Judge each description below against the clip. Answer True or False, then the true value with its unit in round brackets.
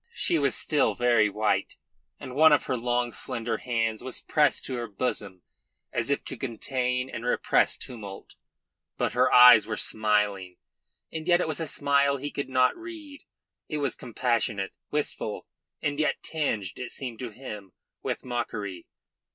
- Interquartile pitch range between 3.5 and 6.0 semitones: True (4.5 semitones)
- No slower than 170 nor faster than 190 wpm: False (160 wpm)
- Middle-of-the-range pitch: False (125 Hz)